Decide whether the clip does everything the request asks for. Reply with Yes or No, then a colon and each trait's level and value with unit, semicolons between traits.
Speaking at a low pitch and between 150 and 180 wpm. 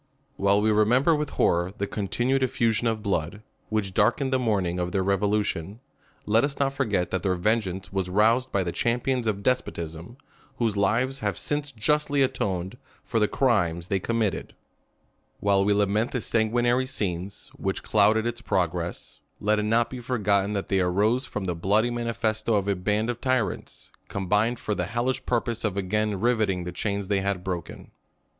Yes: low, 105 Hz; average, 175 wpm